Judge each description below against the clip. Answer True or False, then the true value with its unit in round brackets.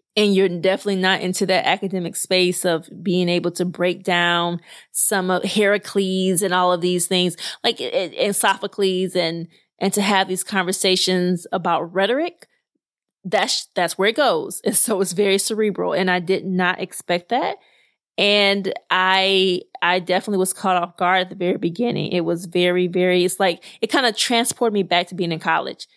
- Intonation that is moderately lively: False (1.6 semitones)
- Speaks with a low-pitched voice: False (185 Hz)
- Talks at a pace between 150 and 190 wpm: True (180 wpm)